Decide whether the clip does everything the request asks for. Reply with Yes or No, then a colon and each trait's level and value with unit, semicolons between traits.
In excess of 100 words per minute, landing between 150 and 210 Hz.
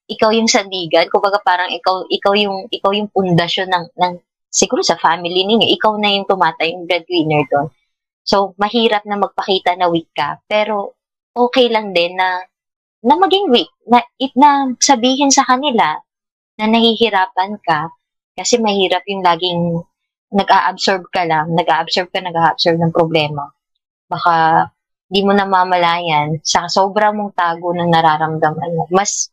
Yes: average, 150 wpm; medium, 185 Hz